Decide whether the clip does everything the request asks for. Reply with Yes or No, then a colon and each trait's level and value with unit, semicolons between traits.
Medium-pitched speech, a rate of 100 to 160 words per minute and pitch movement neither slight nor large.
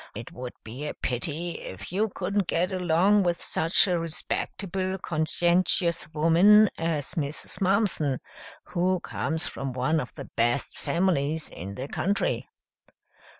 Yes: medium, 170 Hz; slow, 135 wpm; average, 4.3 semitones